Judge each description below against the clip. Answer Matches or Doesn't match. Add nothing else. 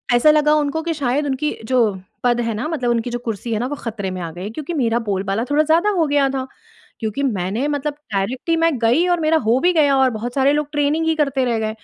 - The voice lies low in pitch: Doesn't match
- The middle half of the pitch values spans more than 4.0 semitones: Matches